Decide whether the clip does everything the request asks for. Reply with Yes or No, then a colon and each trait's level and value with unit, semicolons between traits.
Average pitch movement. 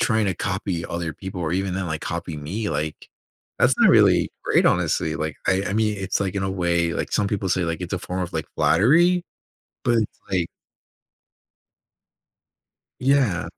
Yes: average, 3.1 semitones